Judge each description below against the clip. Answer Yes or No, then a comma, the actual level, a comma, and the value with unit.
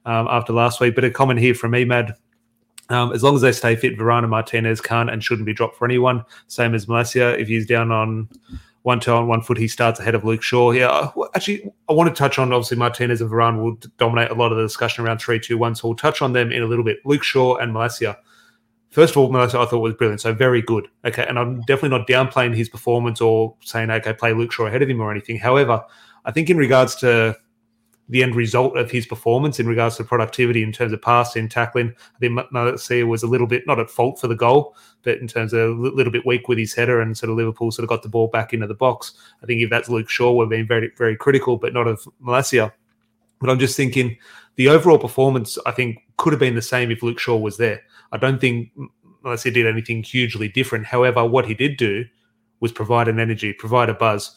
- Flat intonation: Yes, narrow, 1.6 semitones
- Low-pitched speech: Yes, low, 120 Hz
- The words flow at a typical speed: No, fast, 245 wpm